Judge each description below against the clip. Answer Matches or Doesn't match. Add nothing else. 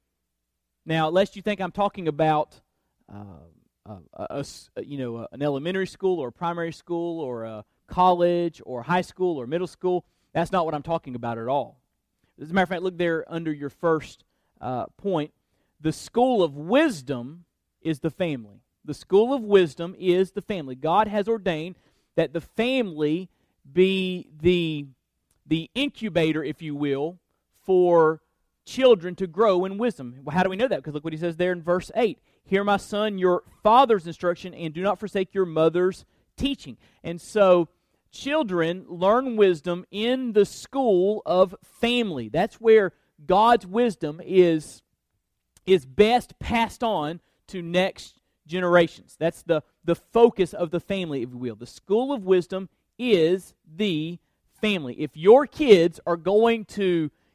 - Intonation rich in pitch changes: Doesn't match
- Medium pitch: Matches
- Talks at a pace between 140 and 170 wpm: Matches